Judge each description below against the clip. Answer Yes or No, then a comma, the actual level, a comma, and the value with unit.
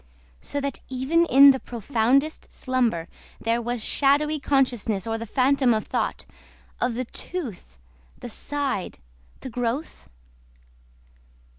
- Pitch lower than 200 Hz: No, very high, 255 Hz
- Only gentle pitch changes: No, average, 3.6 semitones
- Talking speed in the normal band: No, slow, 115 wpm